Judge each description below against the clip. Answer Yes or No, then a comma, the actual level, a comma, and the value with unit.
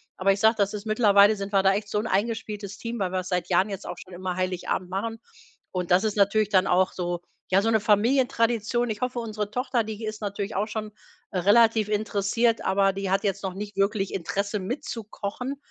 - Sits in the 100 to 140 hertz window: No, high, 205 Hz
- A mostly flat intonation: Yes, narrow, 2.3 semitones